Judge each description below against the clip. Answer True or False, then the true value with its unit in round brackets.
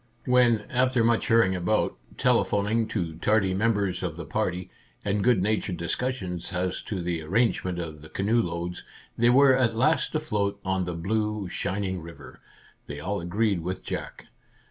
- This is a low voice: True (100 Hz)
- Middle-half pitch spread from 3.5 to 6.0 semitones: True (4.4 semitones)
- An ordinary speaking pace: True (165 wpm)